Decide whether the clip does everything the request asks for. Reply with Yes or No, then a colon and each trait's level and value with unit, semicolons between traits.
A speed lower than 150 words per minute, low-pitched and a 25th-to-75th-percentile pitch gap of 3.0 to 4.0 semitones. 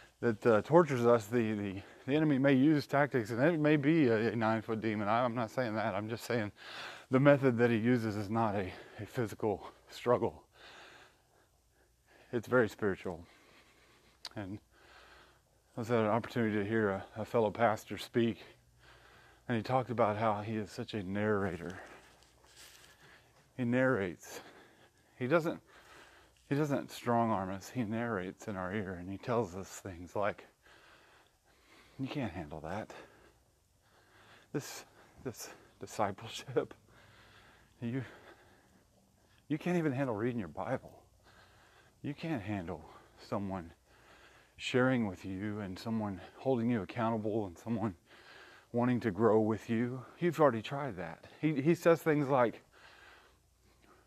Yes: average, 140 wpm; low, 115 Hz; average, 3.7 semitones